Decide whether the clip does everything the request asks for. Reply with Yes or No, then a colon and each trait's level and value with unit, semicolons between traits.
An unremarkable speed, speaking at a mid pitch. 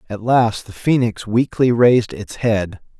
No: average, 160 wpm; low, 115 Hz